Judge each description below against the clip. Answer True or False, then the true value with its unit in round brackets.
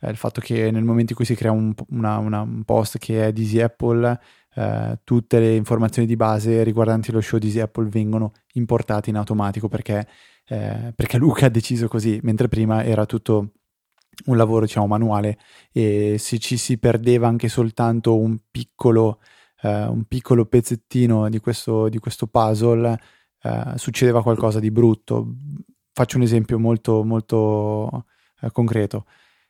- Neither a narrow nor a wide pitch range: False (1.5 semitones)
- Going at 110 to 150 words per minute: False (165 wpm)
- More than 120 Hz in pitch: False (115 Hz)